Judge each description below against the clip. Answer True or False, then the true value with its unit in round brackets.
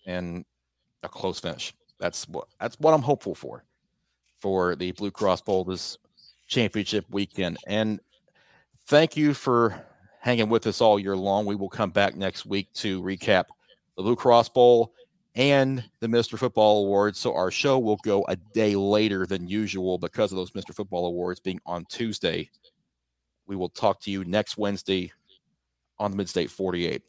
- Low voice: True (100 Hz)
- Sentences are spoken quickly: False (170 wpm)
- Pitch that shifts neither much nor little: True (3.9 semitones)